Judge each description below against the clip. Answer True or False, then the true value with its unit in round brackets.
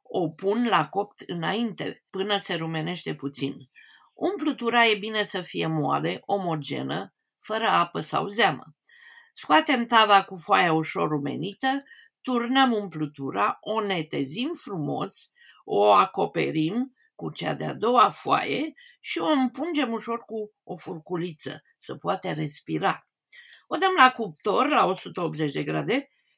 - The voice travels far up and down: True (8.2 semitones)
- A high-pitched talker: True (205 Hz)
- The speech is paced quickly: False (125 wpm)